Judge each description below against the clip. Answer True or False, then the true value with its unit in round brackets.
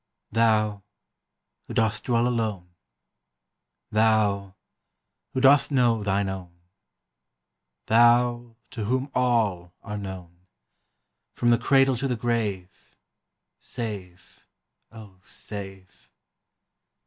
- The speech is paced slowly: True (90 wpm)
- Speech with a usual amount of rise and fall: True (3.6 semitones)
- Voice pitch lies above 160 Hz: False (110 Hz)